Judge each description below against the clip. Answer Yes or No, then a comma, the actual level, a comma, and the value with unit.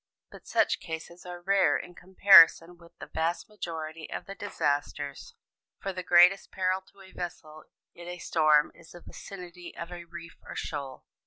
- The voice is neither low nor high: Yes, medium, 175 Hz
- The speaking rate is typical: Yes, average, 170 wpm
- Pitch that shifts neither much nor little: No, narrow, 2.2 semitones